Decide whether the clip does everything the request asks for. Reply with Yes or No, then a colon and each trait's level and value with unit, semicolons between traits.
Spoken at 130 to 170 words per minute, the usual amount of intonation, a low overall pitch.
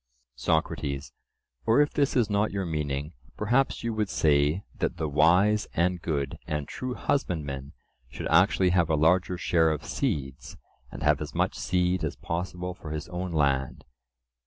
Yes: average, 160 wpm; average, 4.0 semitones; very low, 85 Hz